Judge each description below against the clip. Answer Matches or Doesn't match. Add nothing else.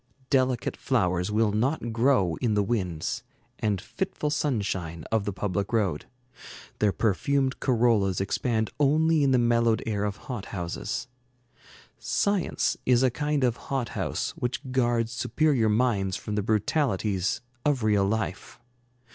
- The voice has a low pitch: Matches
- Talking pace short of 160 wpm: Matches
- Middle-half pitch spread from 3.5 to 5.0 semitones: Matches